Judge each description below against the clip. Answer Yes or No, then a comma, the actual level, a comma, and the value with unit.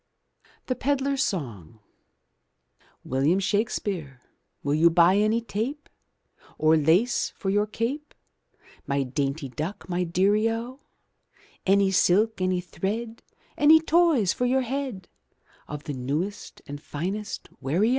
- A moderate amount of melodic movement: No, wide, 6.7 semitones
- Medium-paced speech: No, slow, 125 wpm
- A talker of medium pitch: No, high, 195 Hz